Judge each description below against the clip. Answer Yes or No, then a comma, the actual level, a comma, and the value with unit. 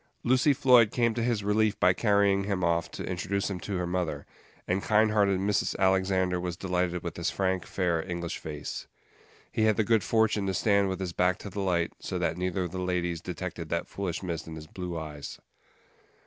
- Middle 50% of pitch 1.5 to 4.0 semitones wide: Yes, narrow, 2.5 semitones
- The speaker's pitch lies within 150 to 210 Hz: No, very low, 95 Hz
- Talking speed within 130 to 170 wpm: No, fast, 205 wpm